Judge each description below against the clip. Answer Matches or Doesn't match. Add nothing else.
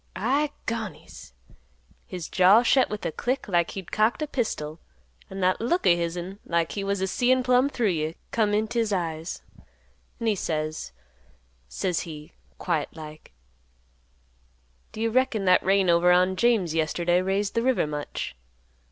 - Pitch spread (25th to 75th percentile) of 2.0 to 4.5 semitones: Doesn't match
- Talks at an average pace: Matches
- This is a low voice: Doesn't match